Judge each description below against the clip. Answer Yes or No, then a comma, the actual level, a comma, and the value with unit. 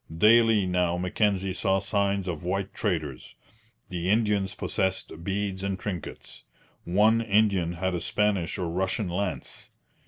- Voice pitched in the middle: No, very low, 95 Hz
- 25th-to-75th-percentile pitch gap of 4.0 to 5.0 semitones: No, narrow, 2.4 semitones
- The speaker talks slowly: Yes, slow, 130 wpm